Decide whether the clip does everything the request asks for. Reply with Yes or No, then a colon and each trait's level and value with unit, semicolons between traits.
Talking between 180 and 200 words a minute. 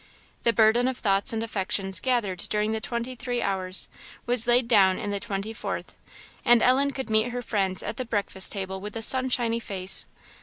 Yes: average, 190 wpm